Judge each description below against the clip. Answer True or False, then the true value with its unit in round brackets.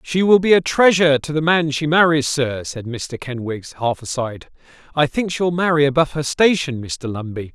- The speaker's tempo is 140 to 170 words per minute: False (200 wpm)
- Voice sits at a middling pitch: True (145 Hz)